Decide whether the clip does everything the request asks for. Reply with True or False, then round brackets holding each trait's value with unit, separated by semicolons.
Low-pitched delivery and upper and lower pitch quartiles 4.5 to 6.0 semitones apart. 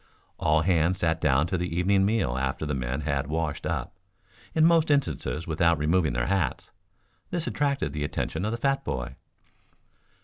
True (80 Hz; 5.1 semitones)